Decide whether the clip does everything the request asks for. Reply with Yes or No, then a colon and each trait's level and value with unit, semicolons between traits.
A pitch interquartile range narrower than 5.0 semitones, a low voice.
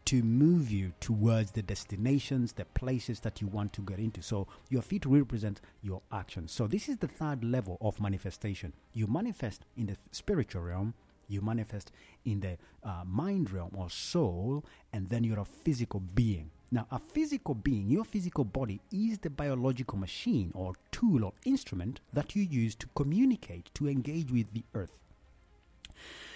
No: wide, 5.4 semitones; low, 110 Hz